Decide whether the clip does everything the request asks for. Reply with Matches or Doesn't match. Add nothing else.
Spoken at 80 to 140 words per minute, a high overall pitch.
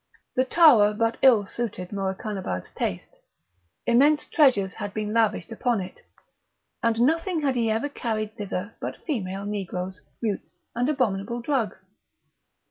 Matches